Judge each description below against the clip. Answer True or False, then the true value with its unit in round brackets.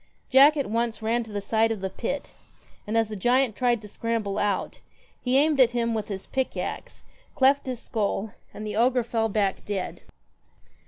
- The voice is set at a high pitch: True (225 Hz)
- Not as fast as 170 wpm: False (195 wpm)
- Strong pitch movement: False (3.1 semitones)